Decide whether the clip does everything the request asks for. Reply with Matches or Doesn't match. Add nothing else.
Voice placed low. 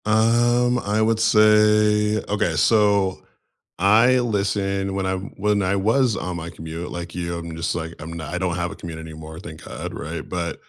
Matches